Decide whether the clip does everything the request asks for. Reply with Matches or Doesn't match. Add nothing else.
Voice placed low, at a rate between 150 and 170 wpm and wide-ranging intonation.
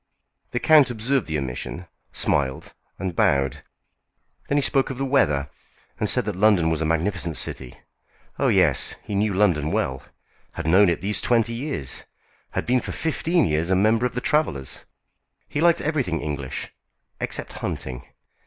Matches